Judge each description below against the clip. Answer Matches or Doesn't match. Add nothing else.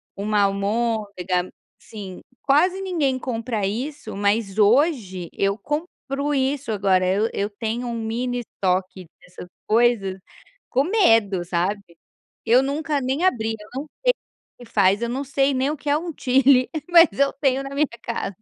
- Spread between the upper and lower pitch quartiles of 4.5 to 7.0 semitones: Matches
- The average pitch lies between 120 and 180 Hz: Doesn't match